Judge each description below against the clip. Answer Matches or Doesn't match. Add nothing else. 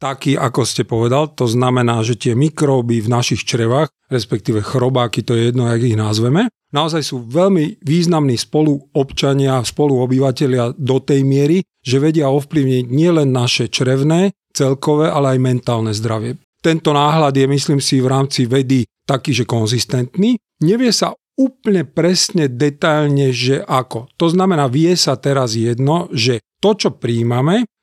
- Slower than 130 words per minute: Doesn't match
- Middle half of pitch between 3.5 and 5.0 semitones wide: Matches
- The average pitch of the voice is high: Doesn't match